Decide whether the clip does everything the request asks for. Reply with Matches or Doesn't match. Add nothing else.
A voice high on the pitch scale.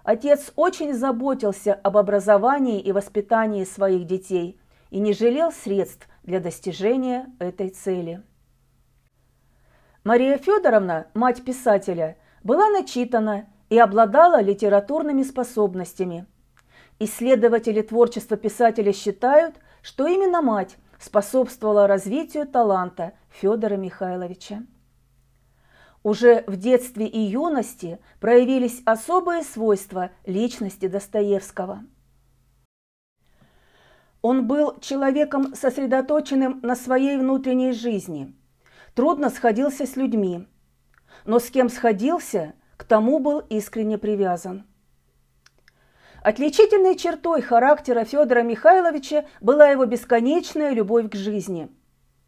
Matches